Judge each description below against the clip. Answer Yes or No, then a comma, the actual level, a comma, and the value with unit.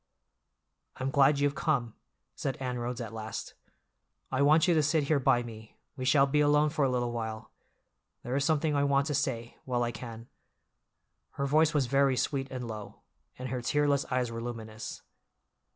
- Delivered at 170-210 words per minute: Yes, average, 180 wpm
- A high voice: No, low, 130 Hz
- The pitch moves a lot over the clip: No, average, 3.2 semitones